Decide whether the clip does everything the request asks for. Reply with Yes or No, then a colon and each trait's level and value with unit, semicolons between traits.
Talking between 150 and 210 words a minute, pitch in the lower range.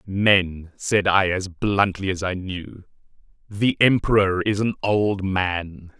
No: average, 140 wpm; very low, 95 Hz